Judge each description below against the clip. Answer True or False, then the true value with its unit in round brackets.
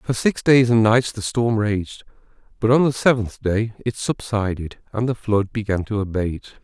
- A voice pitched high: False (110 Hz)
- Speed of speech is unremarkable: True (190 wpm)